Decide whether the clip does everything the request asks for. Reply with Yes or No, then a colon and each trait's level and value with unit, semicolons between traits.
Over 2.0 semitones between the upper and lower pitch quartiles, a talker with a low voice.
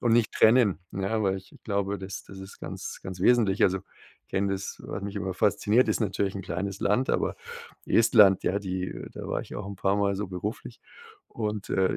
No: narrow, 1.7 semitones; low, 100 Hz